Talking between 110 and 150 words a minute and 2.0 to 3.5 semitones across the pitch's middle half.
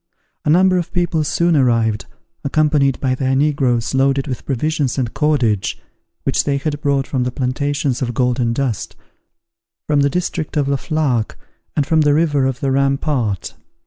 No: average, 170 wpm; average, 3.0 semitones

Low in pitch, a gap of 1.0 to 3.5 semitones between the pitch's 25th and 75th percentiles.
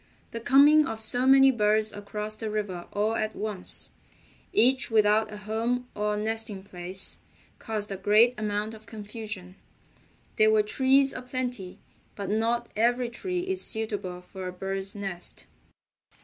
No: high, 215 Hz; average, 2.7 semitones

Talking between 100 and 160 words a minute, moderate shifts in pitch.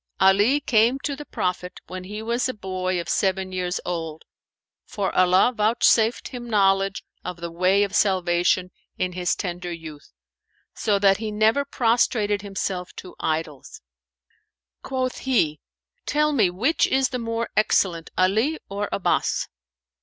Yes: average, 145 wpm; average, 4.0 semitones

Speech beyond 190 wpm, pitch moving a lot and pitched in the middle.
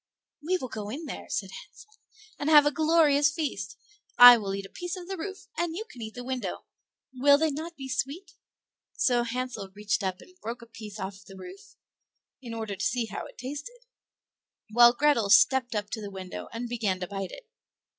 No: fast, 205 wpm; wide, 6.5 semitones; very high, 250 Hz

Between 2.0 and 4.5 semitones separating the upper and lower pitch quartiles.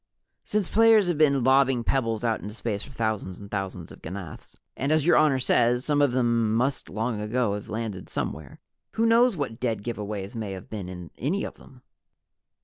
No: average, 5.1 semitones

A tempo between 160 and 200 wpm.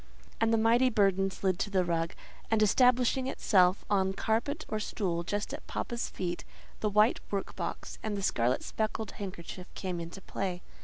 Yes: average, 170 wpm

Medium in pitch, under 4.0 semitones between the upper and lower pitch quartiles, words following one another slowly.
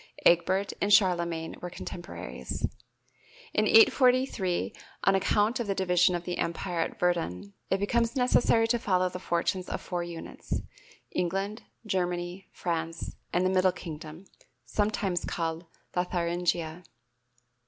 Yes: medium, 180 Hz; narrow, 2.4 semitones; slow, 125 wpm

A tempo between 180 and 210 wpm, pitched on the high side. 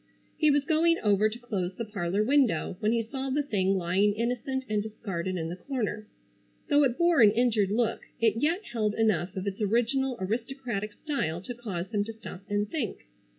Yes: average, 195 wpm; high, 220 Hz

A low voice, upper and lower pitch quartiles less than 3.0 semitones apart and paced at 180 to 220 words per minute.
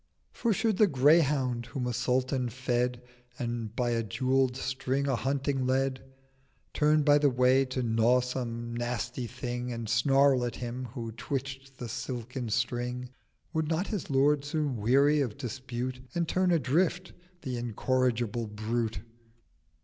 No: low, 125 Hz; narrow, 2.4 semitones; average, 145 wpm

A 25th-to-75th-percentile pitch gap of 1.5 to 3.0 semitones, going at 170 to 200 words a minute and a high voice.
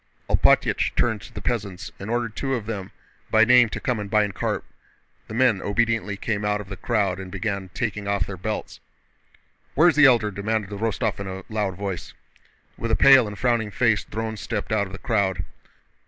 No: narrow, 2.4 semitones; average, 195 wpm; low, 105 Hz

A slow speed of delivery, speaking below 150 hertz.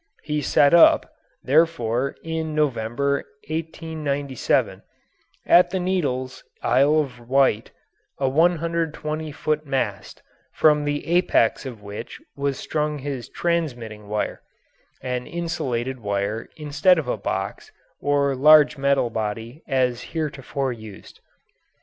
Yes: slow, 115 wpm; medium, 140 Hz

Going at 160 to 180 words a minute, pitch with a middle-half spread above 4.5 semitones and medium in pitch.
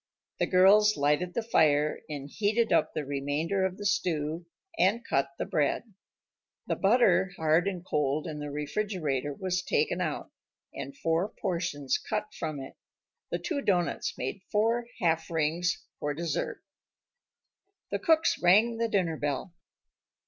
No: average, 145 wpm; wide, 5.5 semitones; medium, 170 Hz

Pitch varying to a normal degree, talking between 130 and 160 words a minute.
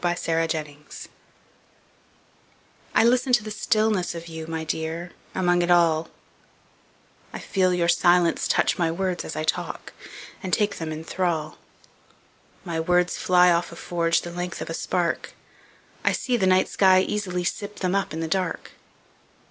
No: narrow, 2.3 semitones; slow, 135 wpm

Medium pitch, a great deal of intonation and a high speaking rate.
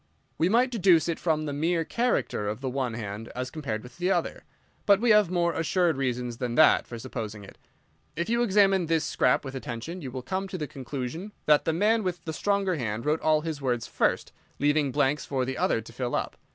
Yes: medium, 150 Hz; wide, 6.1 semitones; fast, 220 wpm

